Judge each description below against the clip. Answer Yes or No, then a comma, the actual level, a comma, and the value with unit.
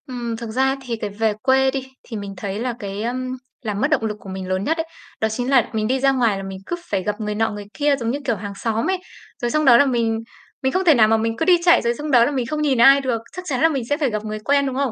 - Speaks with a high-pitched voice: Yes, high, 240 Hz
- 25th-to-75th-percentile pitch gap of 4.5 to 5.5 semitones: No, average, 4.0 semitones